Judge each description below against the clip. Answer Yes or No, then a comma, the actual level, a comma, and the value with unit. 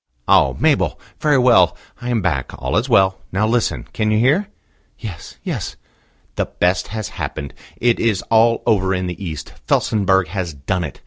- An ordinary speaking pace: Yes, average, 175 wpm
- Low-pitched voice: Yes, very low, 95 Hz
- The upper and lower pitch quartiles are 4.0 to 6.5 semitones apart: Yes, average, 4.3 semitones